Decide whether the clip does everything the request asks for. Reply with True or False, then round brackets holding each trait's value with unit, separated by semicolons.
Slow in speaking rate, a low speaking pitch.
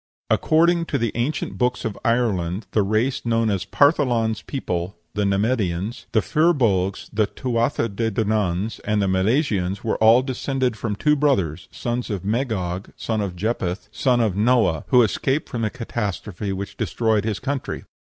False (160 wpm; 110 Hz)